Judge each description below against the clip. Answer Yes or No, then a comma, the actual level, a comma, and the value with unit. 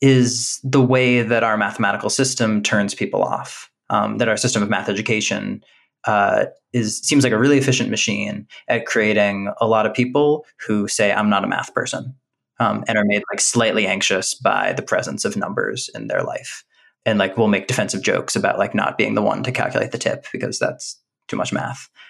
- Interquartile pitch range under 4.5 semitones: Yes, average, 3.9 semitones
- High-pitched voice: No, low, 115 Hz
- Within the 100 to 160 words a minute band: No, average, 200 wpm